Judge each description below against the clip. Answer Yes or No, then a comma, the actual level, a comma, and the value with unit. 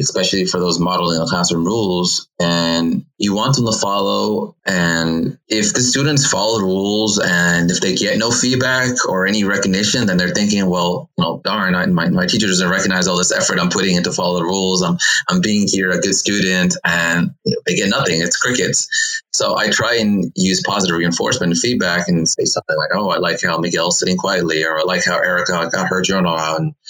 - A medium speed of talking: No, fast, 210 wpm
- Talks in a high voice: No, very low, 95 Hz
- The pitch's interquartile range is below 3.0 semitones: No, average, 3.3 semitones